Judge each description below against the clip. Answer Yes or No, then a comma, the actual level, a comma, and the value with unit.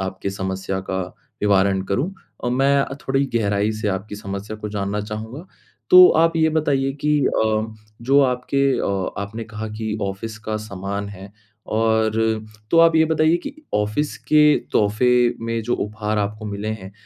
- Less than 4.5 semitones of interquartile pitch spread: No, average, 4.8 semitones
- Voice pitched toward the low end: Yes, low, 110 Hz